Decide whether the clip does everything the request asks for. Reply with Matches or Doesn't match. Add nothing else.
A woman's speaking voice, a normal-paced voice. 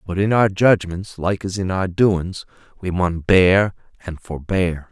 Doesn't match